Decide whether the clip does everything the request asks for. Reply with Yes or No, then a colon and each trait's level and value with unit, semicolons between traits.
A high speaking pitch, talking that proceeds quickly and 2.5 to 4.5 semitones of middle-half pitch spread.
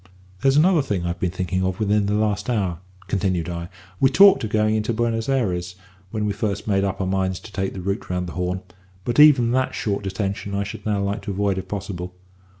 No: low, 100 Hz; fast, 225 wpm; average, 2.8 semitones